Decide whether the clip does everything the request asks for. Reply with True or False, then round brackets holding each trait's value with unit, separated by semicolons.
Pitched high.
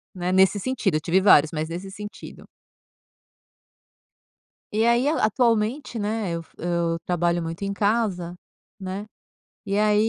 True (195 Hz)